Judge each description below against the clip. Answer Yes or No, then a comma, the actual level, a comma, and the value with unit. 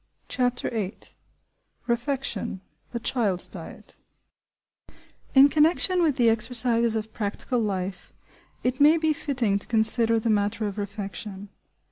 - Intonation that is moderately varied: Yes, average, 3.8 semitones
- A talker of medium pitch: No, high, 230 Hz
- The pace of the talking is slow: Yes, slow, 115 wpm